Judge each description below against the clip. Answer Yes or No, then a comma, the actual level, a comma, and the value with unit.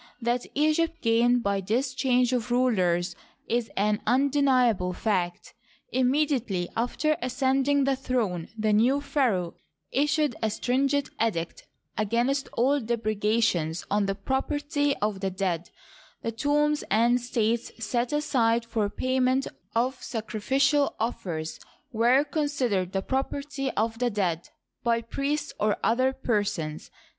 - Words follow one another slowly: Yes, slow, 130 wpm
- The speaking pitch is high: Yes, high, 240 Hz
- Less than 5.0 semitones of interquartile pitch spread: Yes, average, 4.5 semitones